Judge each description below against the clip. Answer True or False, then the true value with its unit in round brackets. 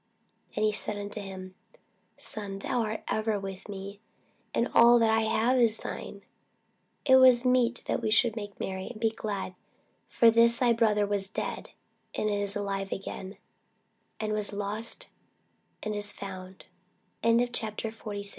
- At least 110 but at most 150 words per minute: True (145 wpm)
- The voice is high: True (215 Hz)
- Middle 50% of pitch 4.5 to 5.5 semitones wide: False (2.5 semitones)